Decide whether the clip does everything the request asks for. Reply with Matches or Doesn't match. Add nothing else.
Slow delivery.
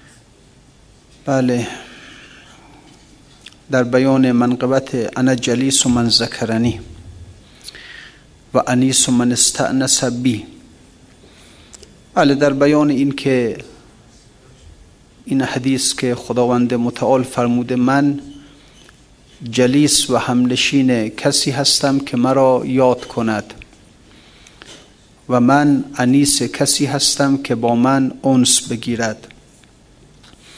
Matches